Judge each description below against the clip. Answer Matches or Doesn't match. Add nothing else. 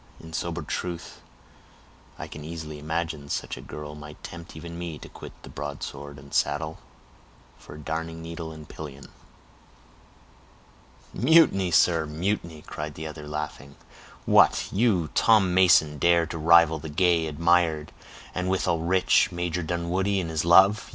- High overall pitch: Doesn't match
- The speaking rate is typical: Matches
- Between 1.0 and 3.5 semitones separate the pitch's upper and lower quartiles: Matches